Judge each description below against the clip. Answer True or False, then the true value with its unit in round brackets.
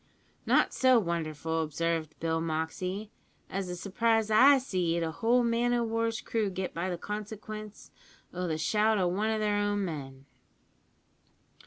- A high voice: True (195 Hz)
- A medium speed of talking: True (150 wpm)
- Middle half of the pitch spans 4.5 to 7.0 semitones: True (4.8 semitones)